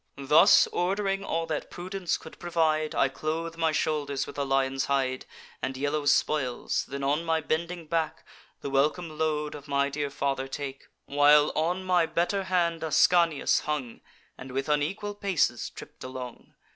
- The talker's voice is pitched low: No, medium, 155 Hz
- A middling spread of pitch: Yes, average, 3.2 semitones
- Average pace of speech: Yes, average, 160 wpm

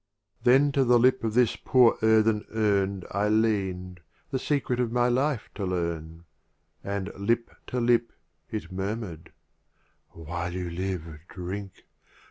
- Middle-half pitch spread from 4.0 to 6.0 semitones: Yes, average, 4.6 semitones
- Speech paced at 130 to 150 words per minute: Yes, average, 145 wpm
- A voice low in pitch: Yes, low, 105 Hz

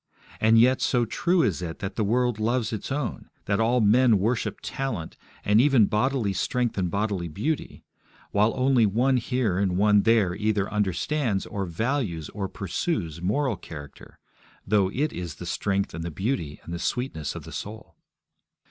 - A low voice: Yes, low, 105 Hz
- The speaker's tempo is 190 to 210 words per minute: No, average, 170 wpm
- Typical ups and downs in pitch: Yes, average, 4.7 semitones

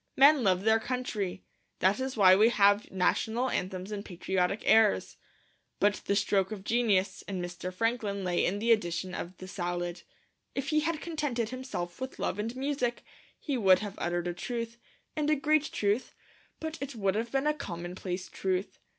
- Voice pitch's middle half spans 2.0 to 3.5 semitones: No, average, 5.2 semitones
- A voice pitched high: Yes, high, 205 Hz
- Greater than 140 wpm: Yes, average, 175 wpm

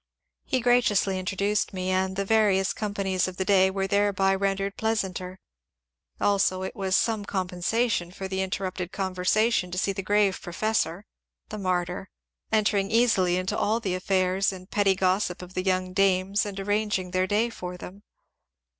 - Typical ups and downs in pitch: No, narrow, 1.8 semitones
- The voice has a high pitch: Yes, high, 195 Hz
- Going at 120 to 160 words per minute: No, average, 170 wpm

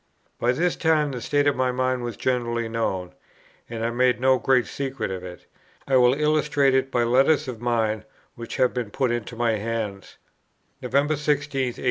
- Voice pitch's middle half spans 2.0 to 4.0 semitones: Yes, average, 2.9 semitones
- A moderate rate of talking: Yes, average, 185 wpm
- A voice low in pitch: Yes, low, 125 Hz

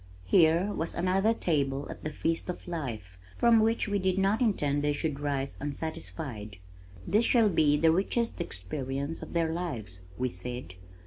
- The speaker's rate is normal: Yes, average, 165 wpm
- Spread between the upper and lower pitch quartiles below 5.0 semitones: No, wide, 5.6 semitones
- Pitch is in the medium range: Yes, medium, 160 Hz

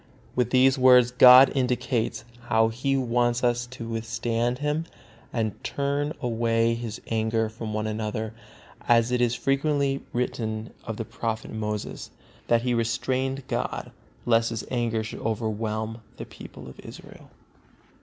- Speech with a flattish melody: Yes, narrow, 2.1 semitones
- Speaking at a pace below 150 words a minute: Yes, average, 140 wpm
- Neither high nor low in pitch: No, low, 115 Hz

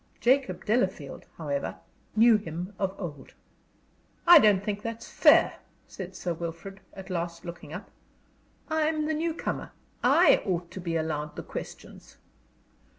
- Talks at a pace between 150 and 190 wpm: No, average, 140 wpm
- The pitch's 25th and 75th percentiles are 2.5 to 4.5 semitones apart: No, wide, 5.4 semitones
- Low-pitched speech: No, high, 190 Hz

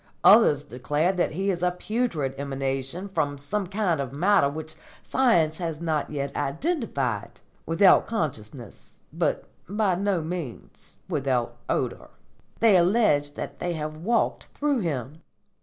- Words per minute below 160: Yes, slow, 135 wpm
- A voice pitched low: No, medium, 160 Hz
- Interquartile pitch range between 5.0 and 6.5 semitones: Yes, wide, 5.5 semitones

